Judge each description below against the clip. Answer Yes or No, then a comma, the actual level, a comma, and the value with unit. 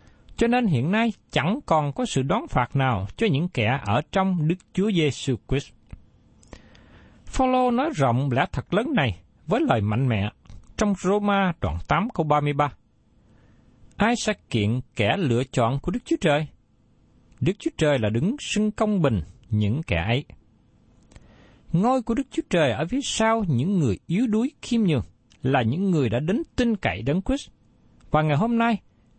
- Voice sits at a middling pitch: Yes, medium, 145 Hz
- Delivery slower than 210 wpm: Yes, average, 175 wpm